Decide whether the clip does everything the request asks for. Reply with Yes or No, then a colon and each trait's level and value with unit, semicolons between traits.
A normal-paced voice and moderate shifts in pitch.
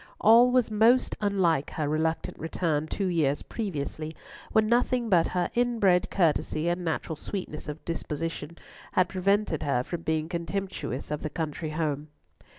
Yes: average, 150 wpm; average, 4.4 semitones